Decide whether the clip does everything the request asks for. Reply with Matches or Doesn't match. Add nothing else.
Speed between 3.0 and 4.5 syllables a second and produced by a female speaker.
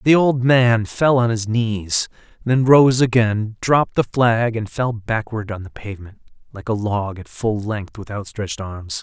Doesn't match